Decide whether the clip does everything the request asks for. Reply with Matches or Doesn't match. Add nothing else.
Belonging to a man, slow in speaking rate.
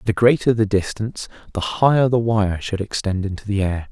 Doesn't match